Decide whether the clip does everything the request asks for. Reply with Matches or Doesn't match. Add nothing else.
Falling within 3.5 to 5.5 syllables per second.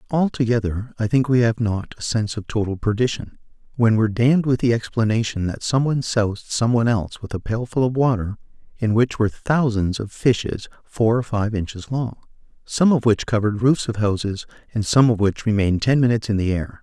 Doesn't match